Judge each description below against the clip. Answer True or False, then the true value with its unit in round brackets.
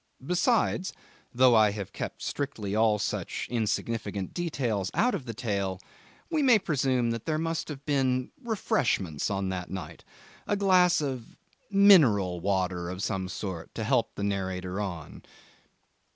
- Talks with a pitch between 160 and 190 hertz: False (115 Hz)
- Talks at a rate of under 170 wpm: True (145 wpm)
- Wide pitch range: True (8.1 semitones)